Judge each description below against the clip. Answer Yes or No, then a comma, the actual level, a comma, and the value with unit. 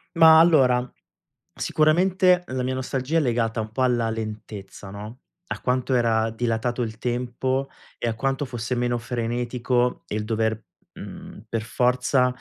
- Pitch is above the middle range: No, low, 125 Hz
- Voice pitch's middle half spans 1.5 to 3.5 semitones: Yes, narrow, 2.4 semitones